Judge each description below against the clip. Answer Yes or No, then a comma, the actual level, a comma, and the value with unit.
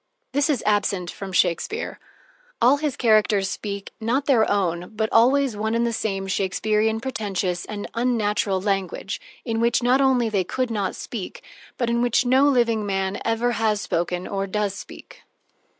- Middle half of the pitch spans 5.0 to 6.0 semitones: No, average, 3.5 semitones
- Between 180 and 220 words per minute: No, average, 165 wpm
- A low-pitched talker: No, high, 220 Hz